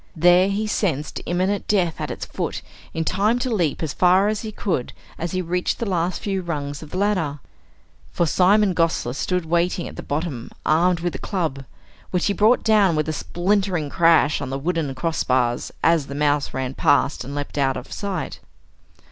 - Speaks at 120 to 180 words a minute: No, average, 190 wpm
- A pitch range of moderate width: Yes, average, 4.5 semitones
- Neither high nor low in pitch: Yes, medium, 170 Hz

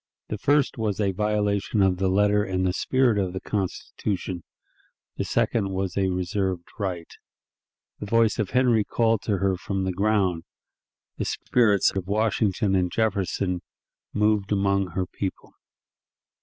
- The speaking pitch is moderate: No, low, 100 Hz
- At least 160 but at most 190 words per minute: No, average, 145 wpm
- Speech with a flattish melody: Yes, narrow, 2.2 semitones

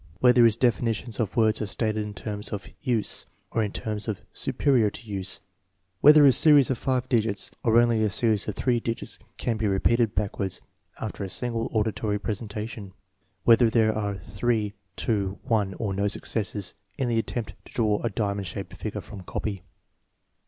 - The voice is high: No, low, 110 Hz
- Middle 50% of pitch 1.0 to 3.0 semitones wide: Yes, narrow, 2.5 semitones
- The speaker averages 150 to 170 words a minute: No, average, 180 wpm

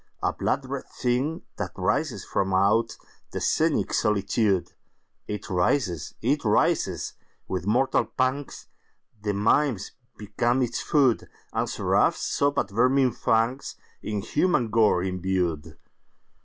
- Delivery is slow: Yes, slow, 95 wpm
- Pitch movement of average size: Yes, average, 4.9 semitones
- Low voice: Yes, low, 115 Hz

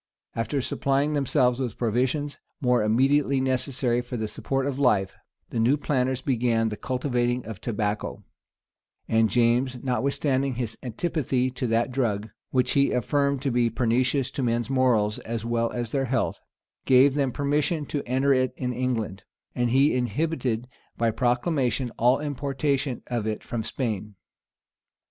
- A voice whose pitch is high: No, low, 125 Hz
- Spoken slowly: No, average, 150 wpm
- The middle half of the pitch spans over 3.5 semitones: No, average, 2.7 semitones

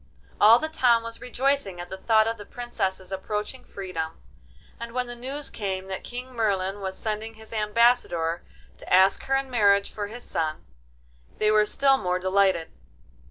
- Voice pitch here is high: Yes, high, 215 Hz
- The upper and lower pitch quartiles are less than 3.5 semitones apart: No, average, 4.1 semitones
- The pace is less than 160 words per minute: No, average, 170 wpm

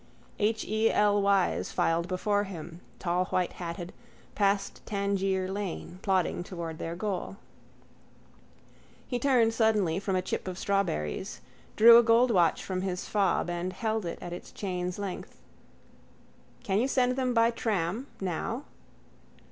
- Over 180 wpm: No, slow, 135 wpm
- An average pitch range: Yes, average, 3.5 semitones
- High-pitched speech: Yes, high, 195 Hz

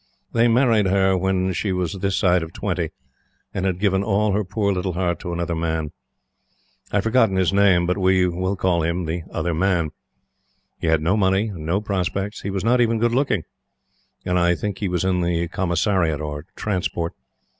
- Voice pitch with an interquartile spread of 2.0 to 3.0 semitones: Yes, narrow, 2.6 semitones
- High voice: No, very low, 95 Hz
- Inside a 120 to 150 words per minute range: No, average, 195 wpm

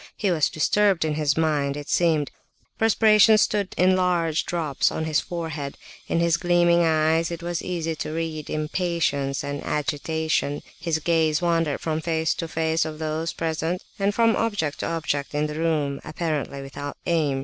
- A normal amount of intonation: No, narrow, 2.1 semitones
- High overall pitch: No, medium, 160 Hz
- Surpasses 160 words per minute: Yes, average, 170 wpm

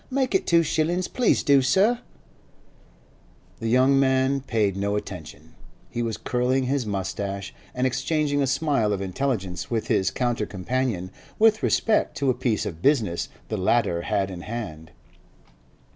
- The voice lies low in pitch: Yes, low, 125 Hz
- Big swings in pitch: Yes, wide, 5.8 semitones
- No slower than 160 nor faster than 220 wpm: No, average, 145 wpm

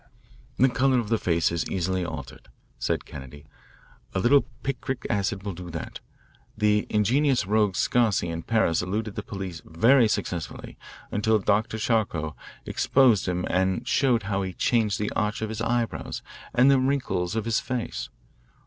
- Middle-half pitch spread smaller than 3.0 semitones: No, average, 4.4 semitones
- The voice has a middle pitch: No, low, 105 Hz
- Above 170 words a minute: No, average, 160 wpm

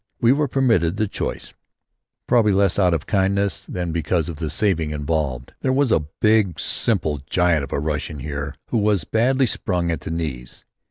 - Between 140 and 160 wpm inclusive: No, average, 180 wpm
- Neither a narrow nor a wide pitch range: No, wide, 5.8 semitones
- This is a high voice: No, very low, 90 Hz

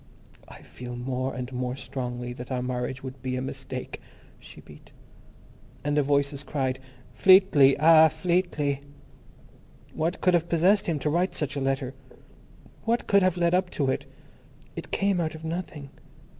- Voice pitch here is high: No, medium, 140 Hz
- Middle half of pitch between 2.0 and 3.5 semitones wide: No, average, 4.7 semitones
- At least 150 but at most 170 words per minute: Yes, average, 165 wpm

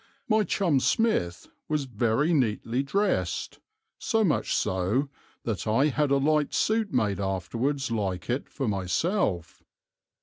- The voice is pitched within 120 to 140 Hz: Yes, low, 135 Hz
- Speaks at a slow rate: Yes, slow, 130 wpm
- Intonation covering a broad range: Yes, wide, 7.0 semitones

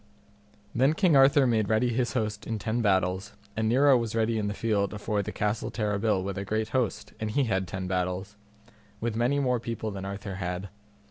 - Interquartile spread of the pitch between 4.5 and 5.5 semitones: No, average, 3.0 semitones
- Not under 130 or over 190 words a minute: No, average, 200 wpm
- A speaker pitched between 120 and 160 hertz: No, low, 110 Hz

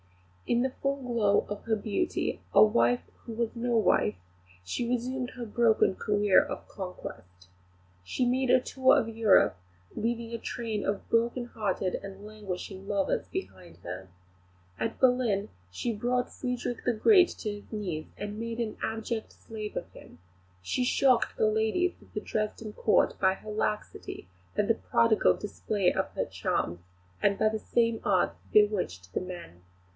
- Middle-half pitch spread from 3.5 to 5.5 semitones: No, average, 3.0 semitones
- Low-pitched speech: No, high, 220 Hz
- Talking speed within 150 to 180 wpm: Yes, average, 160 wpm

